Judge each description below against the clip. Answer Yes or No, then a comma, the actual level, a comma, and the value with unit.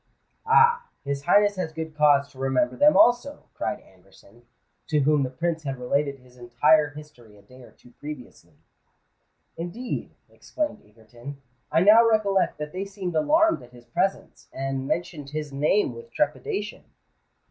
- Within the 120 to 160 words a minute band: Yes, average, 155 wpm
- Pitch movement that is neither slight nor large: No, wide, 7.2 semitones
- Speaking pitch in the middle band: Yes, medium, 150 Hz